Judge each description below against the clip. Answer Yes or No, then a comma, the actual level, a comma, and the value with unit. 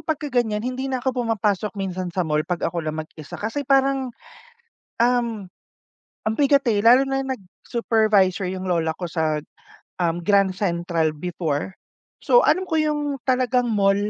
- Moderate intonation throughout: No, wide, 6.5 semitones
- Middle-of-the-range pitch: No, high, 210 Hz